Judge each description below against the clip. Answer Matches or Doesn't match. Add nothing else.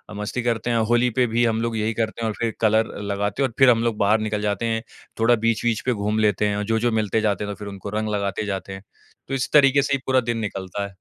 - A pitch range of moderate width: Doesn't match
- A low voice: Matches